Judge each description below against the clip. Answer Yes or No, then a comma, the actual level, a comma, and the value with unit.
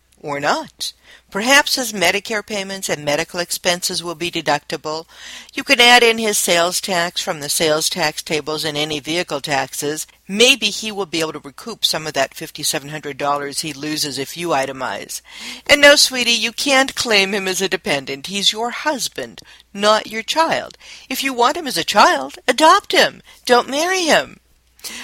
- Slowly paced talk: No, average, 180 wpm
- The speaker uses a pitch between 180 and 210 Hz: Yes, medium, 185 Hz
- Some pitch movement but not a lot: No, wide, 7.7 semitones